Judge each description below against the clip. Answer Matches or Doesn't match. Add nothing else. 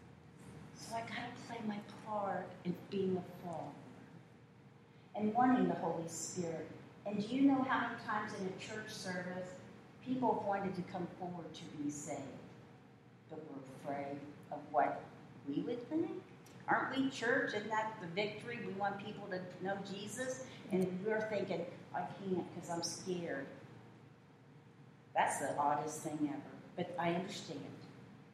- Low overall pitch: Doesn't match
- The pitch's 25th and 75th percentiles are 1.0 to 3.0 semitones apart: Doesn't match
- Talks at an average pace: Matches